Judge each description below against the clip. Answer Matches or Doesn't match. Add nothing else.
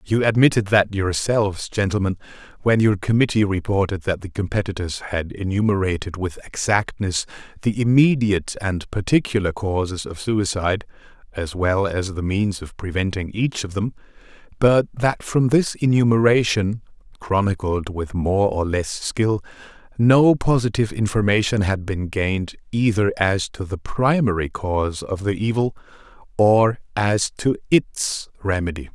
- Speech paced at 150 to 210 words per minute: Doesn't match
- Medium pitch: Doesn't match